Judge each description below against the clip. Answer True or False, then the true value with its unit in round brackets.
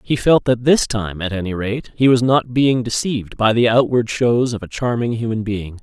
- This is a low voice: True (115 Hz)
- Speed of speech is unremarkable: False (225 wpm)